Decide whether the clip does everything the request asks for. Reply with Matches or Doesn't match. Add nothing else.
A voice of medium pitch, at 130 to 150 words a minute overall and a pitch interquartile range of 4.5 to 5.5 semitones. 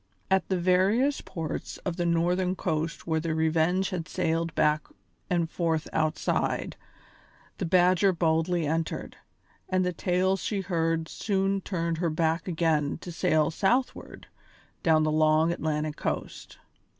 Doesn't match